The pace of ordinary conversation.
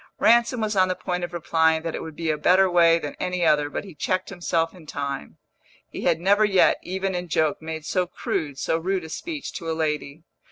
No: fast, 230 wpm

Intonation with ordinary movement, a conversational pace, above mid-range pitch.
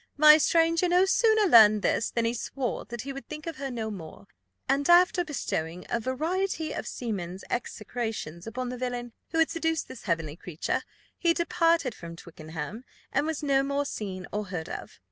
No: wide, 7.8 semitones; average, 185 wpm; very high, 250 Hz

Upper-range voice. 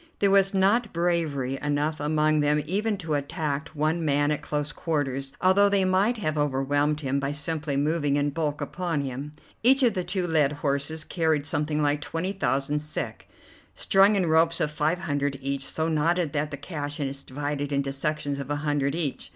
No: medium, 150 Hz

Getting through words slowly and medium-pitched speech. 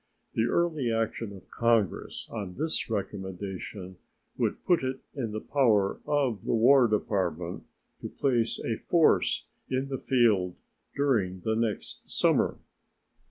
No: slow, 130 wpm; low, 115 Hz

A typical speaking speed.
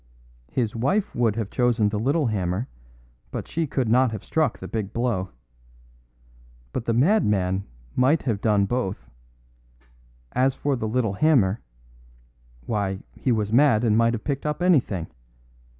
Yes: average, 150 wpm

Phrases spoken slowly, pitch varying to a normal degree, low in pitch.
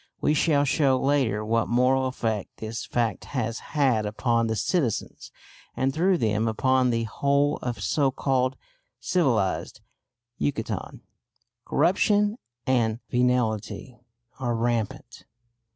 Yes: slow, 115 wpm; average, 3.8 semitones; low, 125 Hz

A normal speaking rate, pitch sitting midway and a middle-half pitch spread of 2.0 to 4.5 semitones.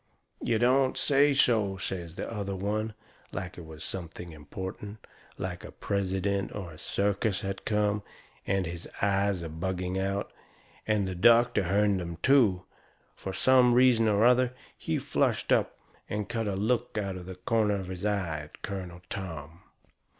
No: average, 165 wpm; low, 100 Hz; average, 2.9 semitones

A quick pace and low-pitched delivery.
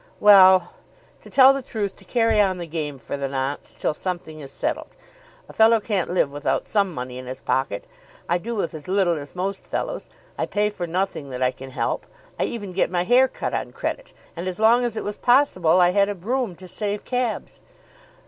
No: fast, 215 wpm; medium, 185 Hz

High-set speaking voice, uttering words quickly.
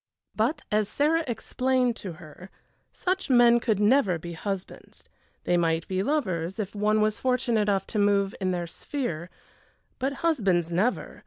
No: high, 210 Hz; average, 155 wpm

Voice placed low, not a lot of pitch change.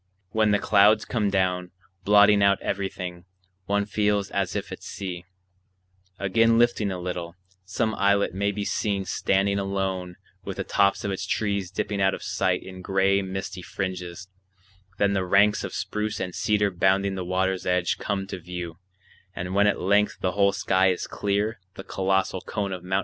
Yes: very low, 95 Hz; narrow, 1.6 semitones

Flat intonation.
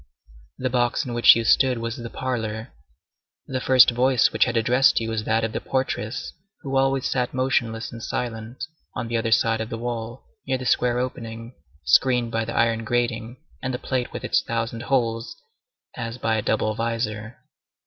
Yes: narrow, 1.9 semitones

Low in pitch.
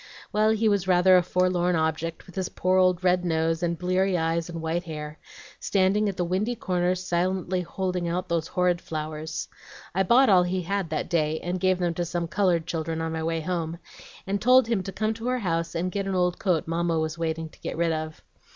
No: medium, 175 Hz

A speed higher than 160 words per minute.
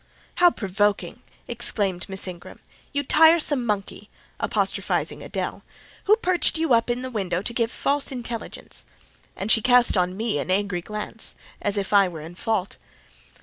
No: average, 155 wpm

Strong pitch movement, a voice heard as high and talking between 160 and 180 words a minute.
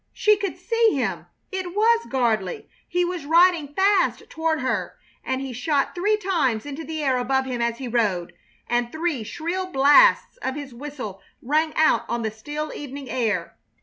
Yes: wide, 6.1 semitones; very high, 290 Hz; average, 175 wpm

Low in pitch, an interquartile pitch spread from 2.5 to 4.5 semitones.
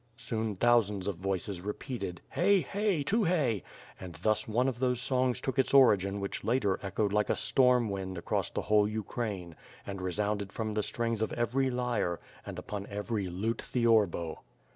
Yes: low, 110 Hz; average, 4.1 semitones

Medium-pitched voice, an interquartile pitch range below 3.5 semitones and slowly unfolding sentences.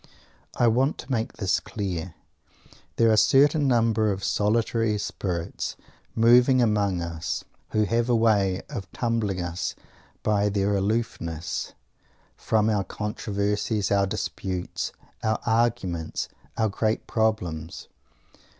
No: low, 105 Hz; average, 3.0 semitones; slow, 120 wpm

